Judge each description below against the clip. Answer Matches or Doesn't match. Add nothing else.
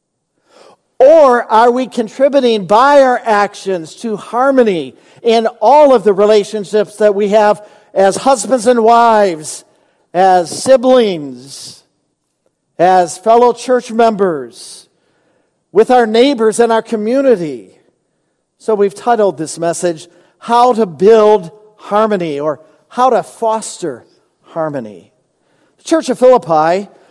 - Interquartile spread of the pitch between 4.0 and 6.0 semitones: Matches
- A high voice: Matches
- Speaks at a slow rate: Matches